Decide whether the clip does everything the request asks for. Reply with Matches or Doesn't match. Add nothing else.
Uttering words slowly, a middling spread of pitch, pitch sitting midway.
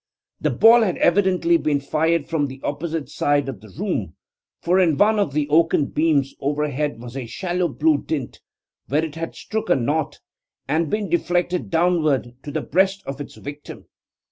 Doesn't match